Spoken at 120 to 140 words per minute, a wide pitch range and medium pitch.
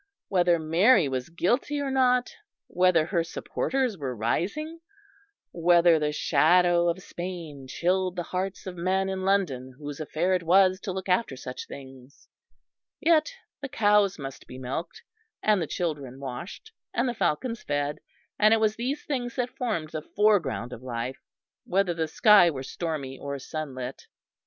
No: average, 155 wpm; wide, 6.1 semitones; medium, 175 Hz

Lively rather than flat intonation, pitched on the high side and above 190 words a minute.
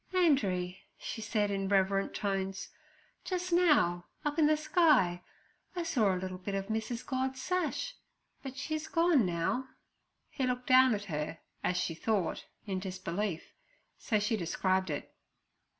No: wide, 7.0 semitones; high, 210 Hz; average, 150 wpm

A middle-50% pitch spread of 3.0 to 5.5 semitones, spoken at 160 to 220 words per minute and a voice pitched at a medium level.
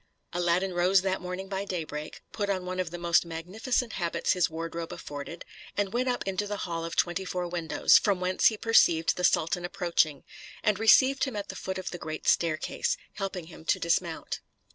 No: narrow, 2.6 semitones; average, 195 wpm; medium, 180 Hz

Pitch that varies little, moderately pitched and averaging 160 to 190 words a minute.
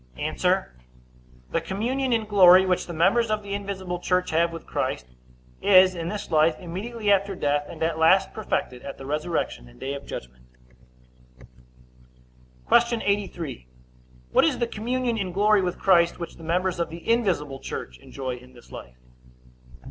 No: average, 4.4 semitones; medium, 180 Hz; average, 165 wpm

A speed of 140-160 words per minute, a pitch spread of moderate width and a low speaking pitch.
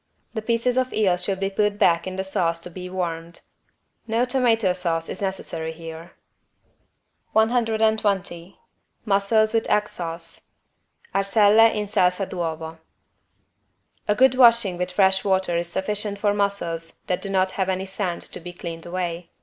No: average, 150 wpm; average, 3.4 semitones; high, 190 Hz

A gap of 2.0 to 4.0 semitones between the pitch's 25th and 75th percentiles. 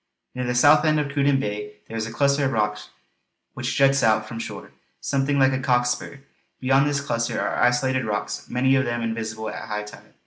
Yes: average, 3.6 semitones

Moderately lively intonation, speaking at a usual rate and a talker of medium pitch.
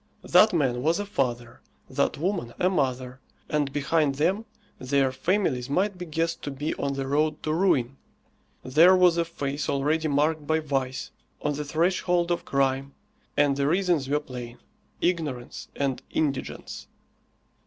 Yes: average, 3.8 semitones; average, 155 wpm; medium, 145 Hz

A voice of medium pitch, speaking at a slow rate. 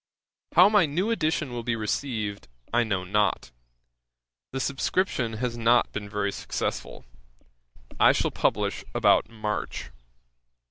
No: low, 120 Hz; slow, 125 wpm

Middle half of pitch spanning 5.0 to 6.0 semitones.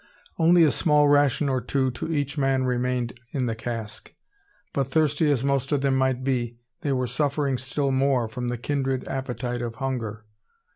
No: narrow, 2.5 semitones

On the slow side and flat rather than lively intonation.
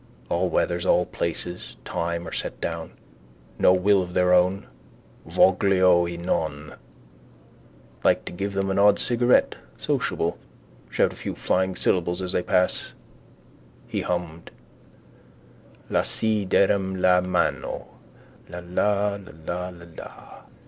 Yes: slow, 125 wpm; narrow, 1.8 semitones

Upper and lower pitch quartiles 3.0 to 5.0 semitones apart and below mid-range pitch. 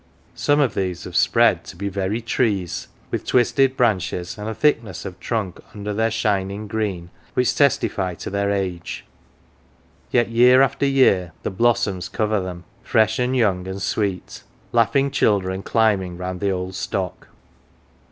Yes: average, 3.7 semitones; low, 100 Hz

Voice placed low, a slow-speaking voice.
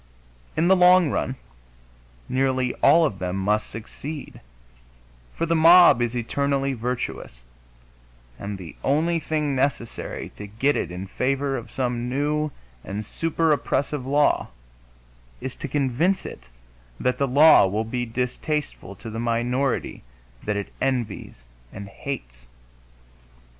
Yes: low, 130 Hz; slow, 130 wpm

